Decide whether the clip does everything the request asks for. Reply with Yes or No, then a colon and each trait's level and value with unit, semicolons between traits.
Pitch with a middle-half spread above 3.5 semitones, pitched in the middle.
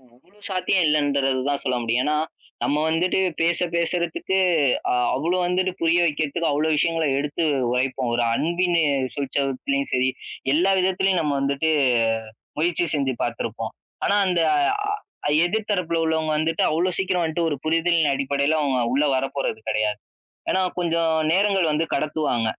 Yes: average, 3.9 semitones; medium, 160 Hz